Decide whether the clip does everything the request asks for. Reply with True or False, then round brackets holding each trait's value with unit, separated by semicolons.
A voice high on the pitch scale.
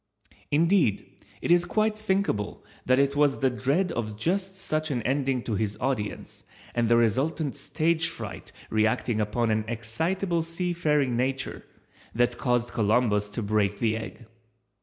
False (130 Hz)